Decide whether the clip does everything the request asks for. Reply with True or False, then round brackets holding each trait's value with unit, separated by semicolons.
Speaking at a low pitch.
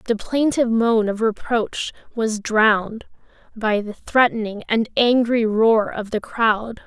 False (225 Hz)